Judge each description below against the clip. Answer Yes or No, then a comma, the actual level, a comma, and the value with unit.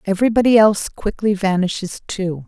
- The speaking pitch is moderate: No, high, 200 Hz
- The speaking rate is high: No, slow, 120 wpm